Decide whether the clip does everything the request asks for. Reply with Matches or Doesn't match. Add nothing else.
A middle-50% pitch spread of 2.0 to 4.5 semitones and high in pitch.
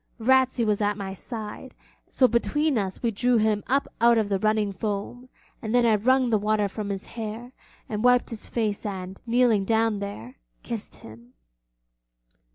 Matches